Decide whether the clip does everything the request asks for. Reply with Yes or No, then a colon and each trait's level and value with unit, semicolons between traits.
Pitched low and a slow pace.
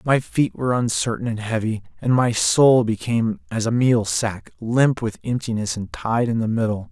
No: low, 115 Hz; average, 190 wpm